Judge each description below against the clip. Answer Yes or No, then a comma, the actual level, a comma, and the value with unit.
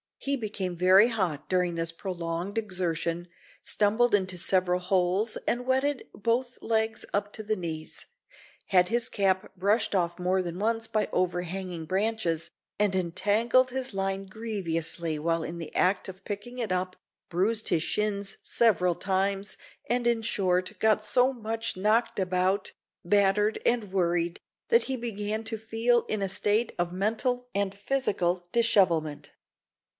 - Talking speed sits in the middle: Yes, average, 145 wpm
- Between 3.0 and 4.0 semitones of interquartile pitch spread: Yes, average, 3.7 semitones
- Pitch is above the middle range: Yes, high, 195 Hz